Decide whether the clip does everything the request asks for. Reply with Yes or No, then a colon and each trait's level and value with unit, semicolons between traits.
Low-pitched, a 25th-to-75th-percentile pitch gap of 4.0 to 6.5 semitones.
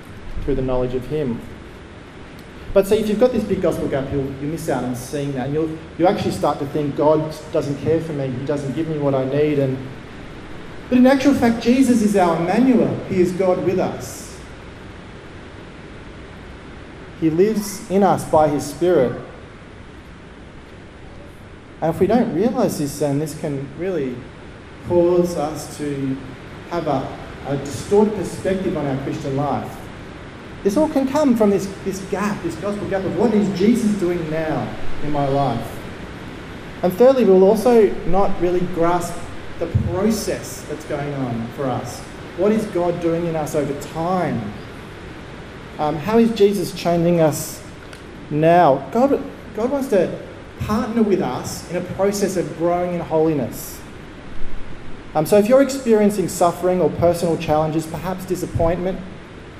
No: medium, 165 Hz; average, 5.3 semitones